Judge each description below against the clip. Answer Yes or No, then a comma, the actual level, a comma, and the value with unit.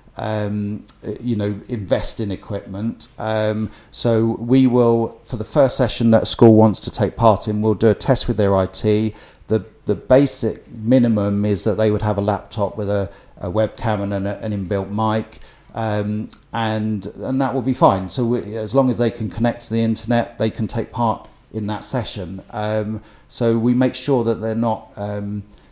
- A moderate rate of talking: Yes, average, 195 wpm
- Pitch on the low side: Yes, low, 110 Hz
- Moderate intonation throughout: No, narrow, 2.1 semitones